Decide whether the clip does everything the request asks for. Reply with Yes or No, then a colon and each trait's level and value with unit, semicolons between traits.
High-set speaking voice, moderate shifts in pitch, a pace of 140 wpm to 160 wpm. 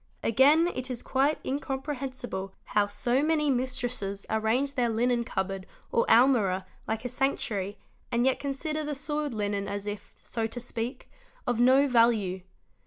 Yes: high, 245 Hz; average, 4.3 semitones; average, 155 wpm